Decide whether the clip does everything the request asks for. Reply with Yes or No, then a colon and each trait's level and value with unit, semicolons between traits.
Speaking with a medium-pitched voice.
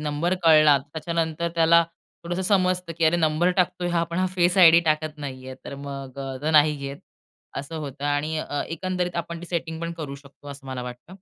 Yes: medium, 160 Hz